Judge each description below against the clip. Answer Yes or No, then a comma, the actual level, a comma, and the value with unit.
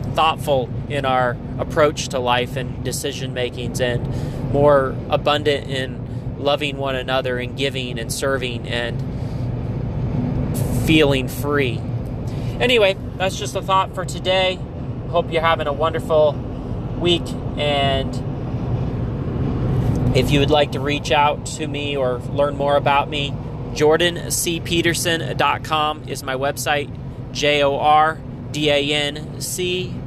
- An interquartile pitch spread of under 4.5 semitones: Yes, narrow, 2.6 semitones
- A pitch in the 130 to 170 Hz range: Yes, low, 135 Hz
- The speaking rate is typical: No, slow, 110 wpm